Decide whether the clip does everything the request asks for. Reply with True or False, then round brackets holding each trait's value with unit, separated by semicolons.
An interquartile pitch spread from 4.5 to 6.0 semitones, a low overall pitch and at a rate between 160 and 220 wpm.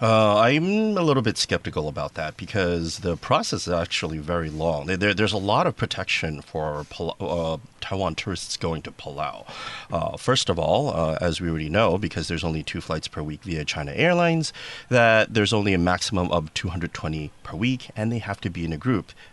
True (5.4 semitones; 95 Hz; 200 wpm)